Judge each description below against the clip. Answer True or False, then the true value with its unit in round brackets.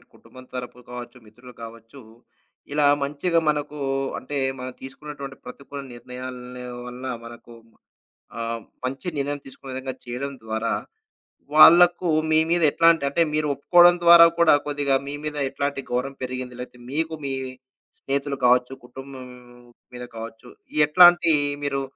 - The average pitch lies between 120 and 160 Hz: True (135 Hz)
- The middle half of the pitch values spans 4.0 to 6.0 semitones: False (3.1 semitones)